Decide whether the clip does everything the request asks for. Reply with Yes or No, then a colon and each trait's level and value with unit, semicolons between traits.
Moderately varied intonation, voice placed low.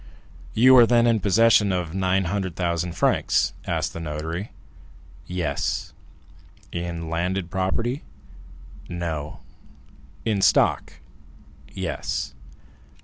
Yes: average, 3.5 semitones; very low, 90 Hz